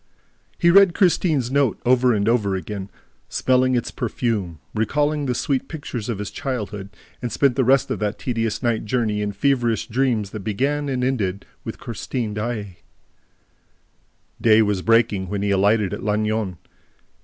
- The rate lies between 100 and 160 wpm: Yes, average, 155 wpm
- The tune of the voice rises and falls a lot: No, average, 3.9 semitones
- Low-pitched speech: Yes, low, 115 Hz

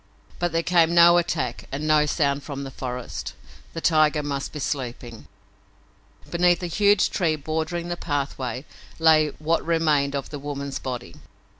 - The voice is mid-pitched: Yes, medium, 155 Hz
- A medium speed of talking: Yes, average, 155 wpm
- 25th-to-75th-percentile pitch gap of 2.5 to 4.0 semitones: Yes, average, 3.1 semitones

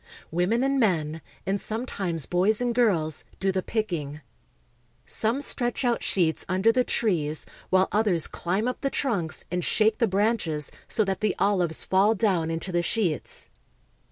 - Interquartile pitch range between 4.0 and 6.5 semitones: Yes, average, 4.7 semitones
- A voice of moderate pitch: No, high, 195 Hz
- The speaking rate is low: No, average, 155 wpm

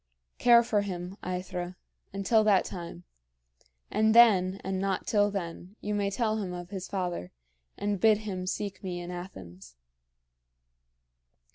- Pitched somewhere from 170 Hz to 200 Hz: Yes, high, 190 Hz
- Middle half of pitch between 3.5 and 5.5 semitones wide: No, narrow, 2.5 semitones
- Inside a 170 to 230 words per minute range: No, average, 140 wpm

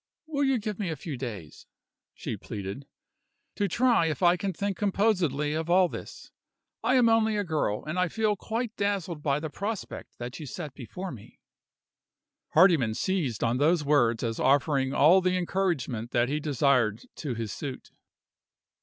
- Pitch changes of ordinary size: No, wide, 7.0 semitones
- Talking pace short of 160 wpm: No, average, 170 wpm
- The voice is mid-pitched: Yes, medium, 160 Hz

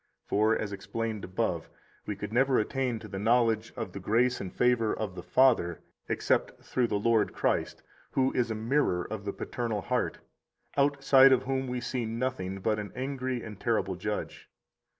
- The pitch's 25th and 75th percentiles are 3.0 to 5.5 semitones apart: Yes, average, 3.4 semitones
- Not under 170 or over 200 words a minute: Yes, average, 180 wpm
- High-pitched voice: No, low, 115 Hz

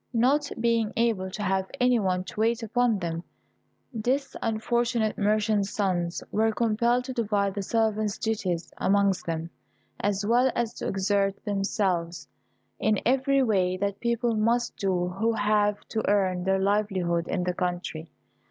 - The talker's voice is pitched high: Yes, high, 210 Hz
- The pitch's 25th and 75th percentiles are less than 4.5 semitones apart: Yes, average, 3.3 semitones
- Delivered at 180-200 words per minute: No, average, 150 wpm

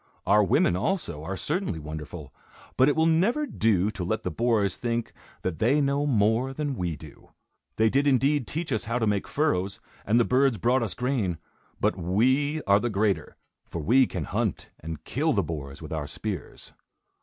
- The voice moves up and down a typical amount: No, wide, 7.1 semitones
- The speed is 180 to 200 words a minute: Yes, average, 190 wpm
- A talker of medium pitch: No, low, 110 Hz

